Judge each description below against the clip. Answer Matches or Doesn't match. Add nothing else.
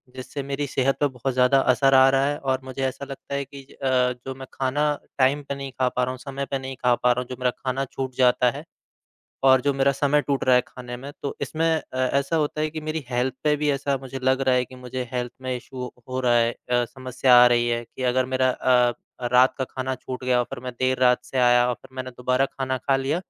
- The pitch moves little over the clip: Matches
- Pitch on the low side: Matches